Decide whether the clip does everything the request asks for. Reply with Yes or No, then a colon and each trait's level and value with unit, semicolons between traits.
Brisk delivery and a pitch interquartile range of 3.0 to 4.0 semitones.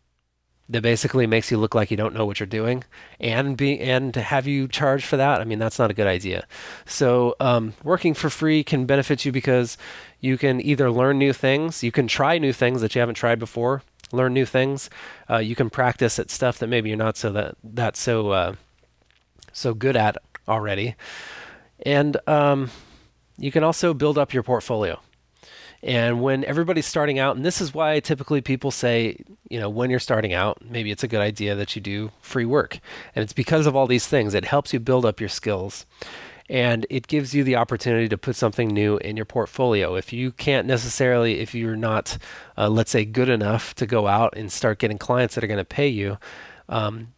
Yes: fast, 210 wpm; average, 3.7 semitones